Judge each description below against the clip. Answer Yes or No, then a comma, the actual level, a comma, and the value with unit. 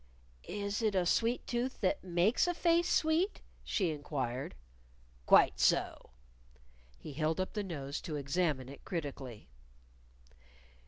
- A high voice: No, medium, 175 Hz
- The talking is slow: Yes, slow, 125 wpm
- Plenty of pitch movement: Yes, wide, 8.1 semitones